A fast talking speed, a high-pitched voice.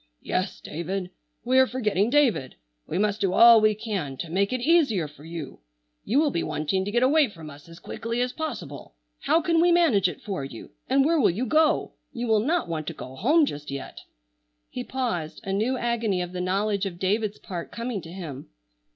Yes: fast, 210 wpm; high, 210 Hz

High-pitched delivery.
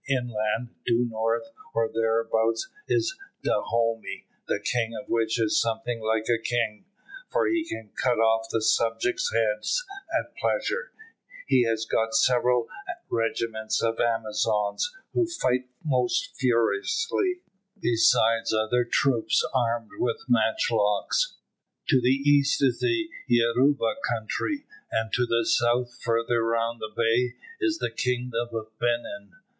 No: low, 115 Hz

